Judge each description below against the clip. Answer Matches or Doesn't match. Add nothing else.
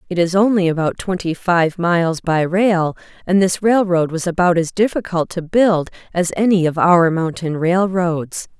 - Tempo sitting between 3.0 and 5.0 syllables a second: Matches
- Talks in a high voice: Doesn't match